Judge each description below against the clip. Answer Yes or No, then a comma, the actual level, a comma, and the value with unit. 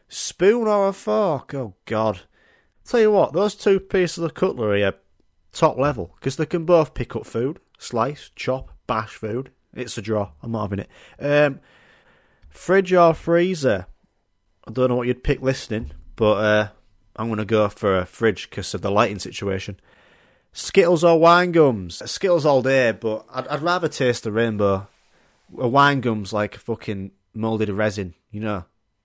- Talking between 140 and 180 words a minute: Yes, average, 175 wpm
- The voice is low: Yes, low, 120 Hz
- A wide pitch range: Yes, wide, 7.1 semitones